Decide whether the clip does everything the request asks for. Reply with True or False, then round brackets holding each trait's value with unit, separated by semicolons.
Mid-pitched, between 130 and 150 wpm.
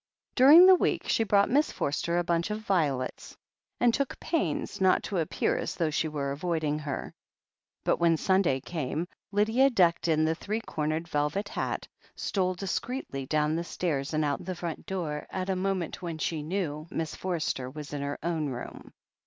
False (170 Hz; 185 wpm)